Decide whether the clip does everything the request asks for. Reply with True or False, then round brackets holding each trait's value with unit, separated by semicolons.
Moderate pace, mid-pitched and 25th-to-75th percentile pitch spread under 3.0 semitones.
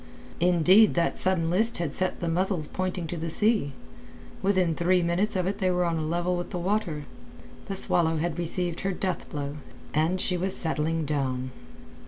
True (185 wpm; 175 Hz; 2.5 semitones)